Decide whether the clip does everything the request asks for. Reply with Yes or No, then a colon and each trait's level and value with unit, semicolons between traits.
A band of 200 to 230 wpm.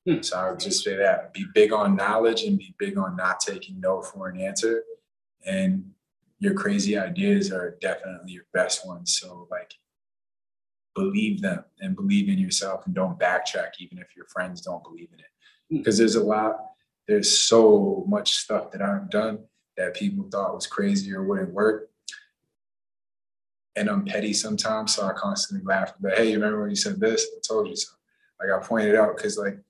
No: average, 190 wpm